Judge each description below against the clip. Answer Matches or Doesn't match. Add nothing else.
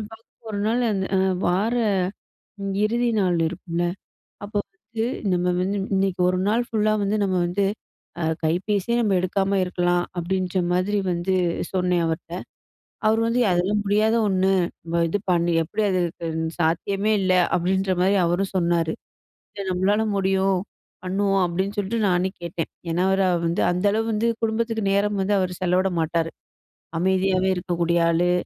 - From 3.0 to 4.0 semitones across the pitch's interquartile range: Doesn't match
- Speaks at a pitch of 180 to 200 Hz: Matches